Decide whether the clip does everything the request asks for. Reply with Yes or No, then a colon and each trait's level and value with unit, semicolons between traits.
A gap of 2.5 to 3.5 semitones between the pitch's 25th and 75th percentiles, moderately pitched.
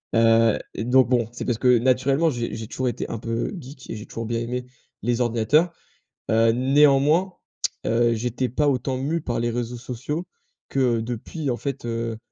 No: average, 2.8 semitones; low, 120 Hz